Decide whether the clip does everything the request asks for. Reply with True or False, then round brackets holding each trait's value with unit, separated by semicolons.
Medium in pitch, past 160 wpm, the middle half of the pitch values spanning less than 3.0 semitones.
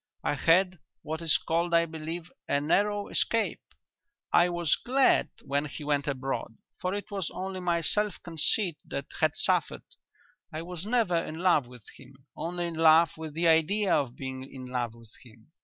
False (165 Hz; 175 wpm; 4.1 semitones)